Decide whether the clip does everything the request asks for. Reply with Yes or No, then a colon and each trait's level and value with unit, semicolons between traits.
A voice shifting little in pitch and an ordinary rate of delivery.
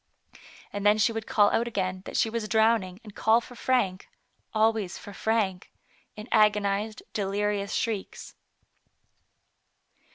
No: narrow, 1.9 semitones; slow, 130 wpm